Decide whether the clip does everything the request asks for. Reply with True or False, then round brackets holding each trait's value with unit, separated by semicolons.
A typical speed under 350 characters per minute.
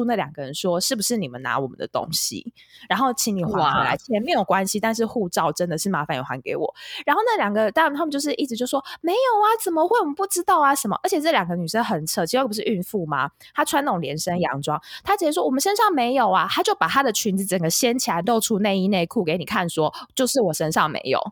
False (375 characters per minute)